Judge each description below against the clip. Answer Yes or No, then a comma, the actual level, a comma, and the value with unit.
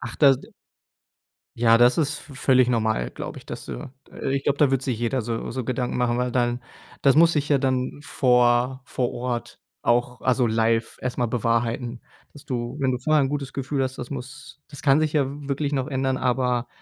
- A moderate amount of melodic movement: No, narrow, 2.2 semitones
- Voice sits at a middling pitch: No, low, 130 Hz